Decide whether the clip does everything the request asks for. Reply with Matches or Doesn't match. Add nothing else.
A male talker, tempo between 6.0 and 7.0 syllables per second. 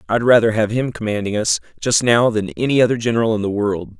Matches